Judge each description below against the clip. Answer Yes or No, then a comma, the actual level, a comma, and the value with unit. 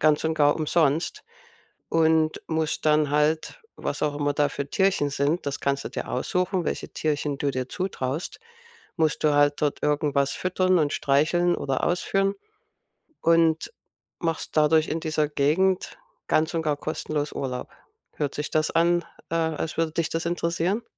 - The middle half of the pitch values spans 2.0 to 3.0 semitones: Yes, narrow, 2.5 semitones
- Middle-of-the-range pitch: Yes, medium, 155 Hz